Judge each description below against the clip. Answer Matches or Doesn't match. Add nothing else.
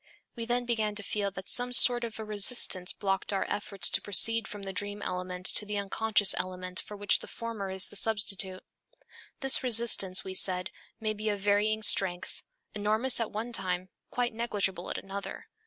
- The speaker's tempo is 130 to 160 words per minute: Doesn't match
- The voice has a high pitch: Matches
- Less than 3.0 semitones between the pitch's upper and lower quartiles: Matches